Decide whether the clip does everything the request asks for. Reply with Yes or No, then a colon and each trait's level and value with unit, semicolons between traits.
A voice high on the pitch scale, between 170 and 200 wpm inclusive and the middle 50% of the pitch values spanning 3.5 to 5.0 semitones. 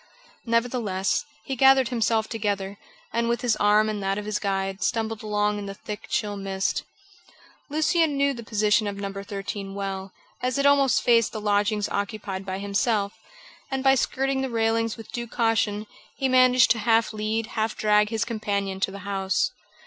No: high, 215 Hz; average, 175 wpm; average, 2.8 semitones